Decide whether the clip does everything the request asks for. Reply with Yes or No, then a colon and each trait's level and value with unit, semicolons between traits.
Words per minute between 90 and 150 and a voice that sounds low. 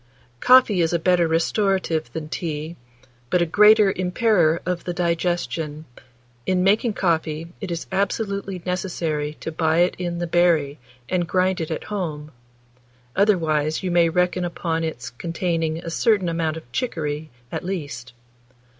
No: average, 145 wpm; medium, 170 Hz